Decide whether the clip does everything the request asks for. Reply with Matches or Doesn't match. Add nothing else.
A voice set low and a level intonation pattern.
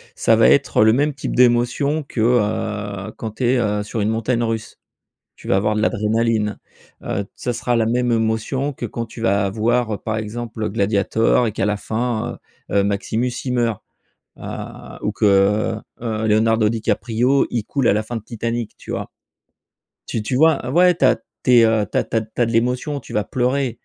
Matches